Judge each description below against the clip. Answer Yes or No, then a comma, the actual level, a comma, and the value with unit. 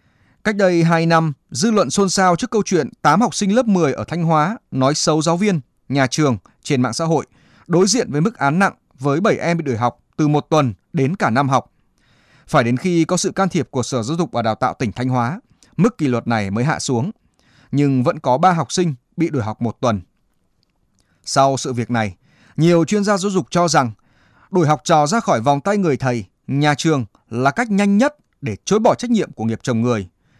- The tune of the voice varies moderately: No, wide, 6.4 semitones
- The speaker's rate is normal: Yes, average, 235 wpm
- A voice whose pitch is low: No, medium, 150 Hz